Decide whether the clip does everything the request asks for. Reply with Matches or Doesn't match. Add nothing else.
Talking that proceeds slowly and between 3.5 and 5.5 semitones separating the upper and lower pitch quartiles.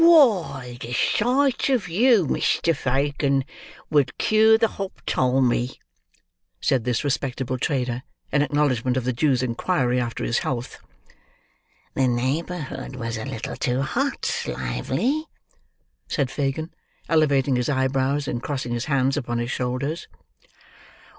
Matches